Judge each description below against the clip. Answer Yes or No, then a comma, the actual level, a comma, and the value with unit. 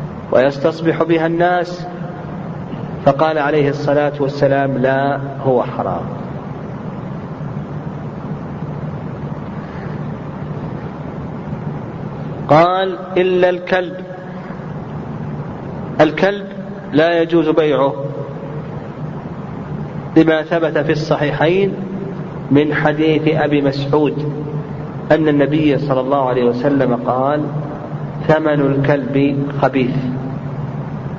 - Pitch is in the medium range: Yes, medium, 150 Hz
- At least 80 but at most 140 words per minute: No, slow, 65 wpm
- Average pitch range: Yes, average, 3.4 semitones